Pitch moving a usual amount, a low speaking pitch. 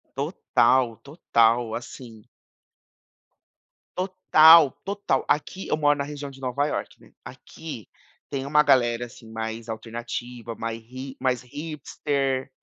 Yes: average, 3.9 semitones; low, 130 Hz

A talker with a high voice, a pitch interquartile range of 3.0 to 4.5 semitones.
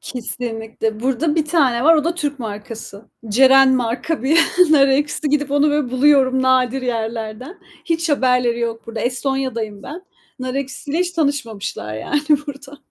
Yes: very high, 260 Hz; average, 3.9 semitones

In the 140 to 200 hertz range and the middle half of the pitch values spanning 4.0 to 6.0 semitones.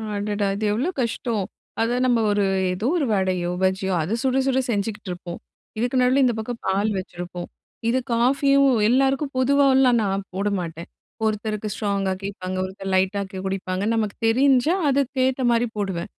No: high, 215 Hz; average, 5.0 semitones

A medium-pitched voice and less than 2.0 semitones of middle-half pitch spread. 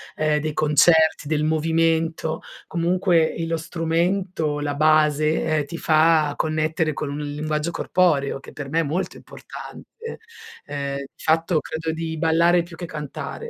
Yes: medium, 160 Hz; narrow, 1.6 semitones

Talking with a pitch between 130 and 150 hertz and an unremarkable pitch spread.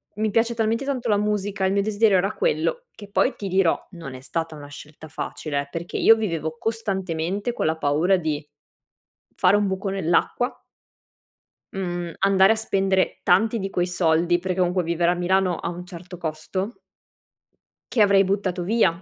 No: high, 190 Hz; average, 3.3 semitones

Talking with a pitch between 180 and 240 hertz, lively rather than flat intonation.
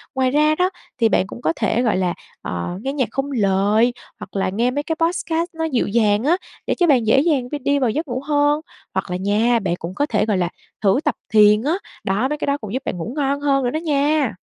No: very high, 255 Hz; wide, 5.7 semitones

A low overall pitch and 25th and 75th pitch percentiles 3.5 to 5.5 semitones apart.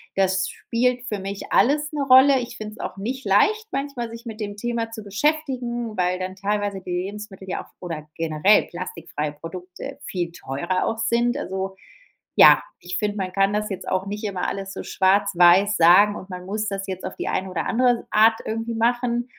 No: high, 205 Hz; average, 4.0 semitones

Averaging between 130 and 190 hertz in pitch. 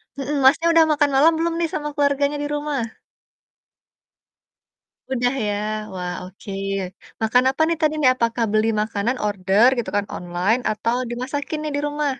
No: very high, 260 Hz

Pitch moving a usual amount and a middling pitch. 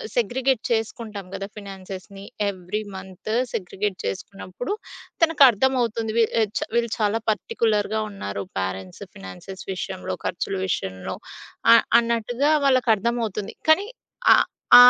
No: average, 3.9 semitones; high, 210 Hz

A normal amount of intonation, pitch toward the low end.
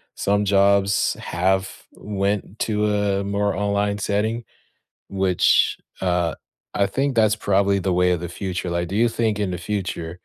No: narrow, 1.8 semitones; low, 100 Hz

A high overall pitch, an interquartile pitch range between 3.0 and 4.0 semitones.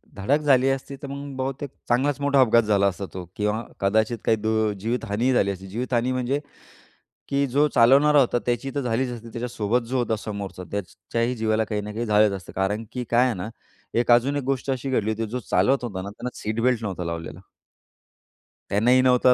No: low, 120 Hz; average, 3.6 semitones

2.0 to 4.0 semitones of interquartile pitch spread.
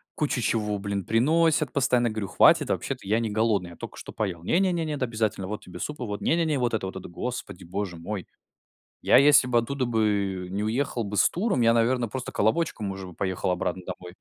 No: average, 4.7 semitones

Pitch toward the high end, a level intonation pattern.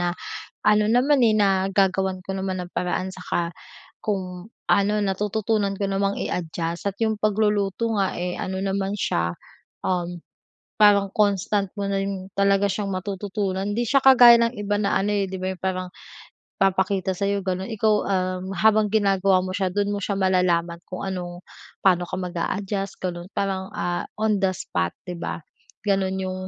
Yes: high, 195 Hz; narrow, 1.8 semitones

